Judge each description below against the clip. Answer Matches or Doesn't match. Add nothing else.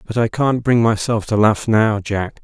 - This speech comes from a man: Matches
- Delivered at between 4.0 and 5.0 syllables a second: Matches